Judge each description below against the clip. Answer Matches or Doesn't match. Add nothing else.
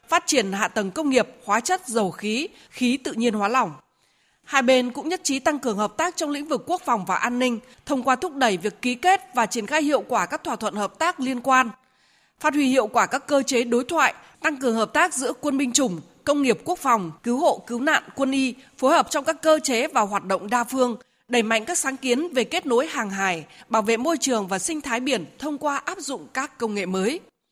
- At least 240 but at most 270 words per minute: Matches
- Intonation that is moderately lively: Matches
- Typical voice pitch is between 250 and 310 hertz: Matches